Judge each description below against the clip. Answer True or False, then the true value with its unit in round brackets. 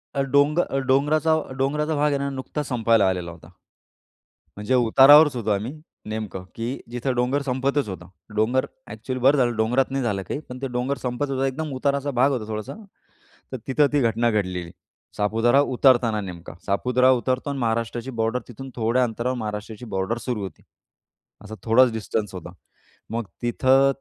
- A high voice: False (125 Hz)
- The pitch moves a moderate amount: True (3.6 semitones)